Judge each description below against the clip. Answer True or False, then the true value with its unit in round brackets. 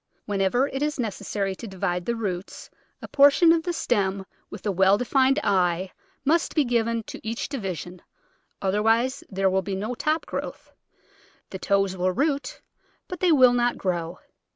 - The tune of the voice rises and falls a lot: True (5.7 semitones)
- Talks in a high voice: True (210 Hz)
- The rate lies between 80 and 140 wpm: False (170 wpm)